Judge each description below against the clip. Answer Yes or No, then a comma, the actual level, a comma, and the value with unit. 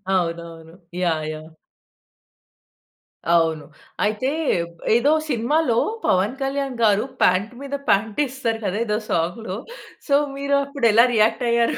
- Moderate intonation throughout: No, wide, 6.7 semitones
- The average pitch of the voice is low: No, high, 220 Hz